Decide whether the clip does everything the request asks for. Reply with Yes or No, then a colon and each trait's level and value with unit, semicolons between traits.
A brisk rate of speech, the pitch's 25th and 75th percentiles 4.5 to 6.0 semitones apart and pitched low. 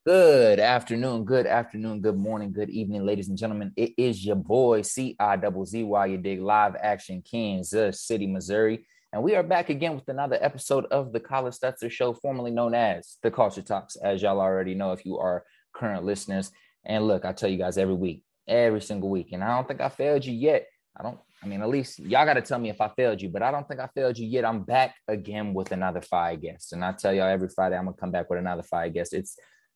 Yes: fast, 235 wpm; average, 4.8 semitones; low, 105 Hz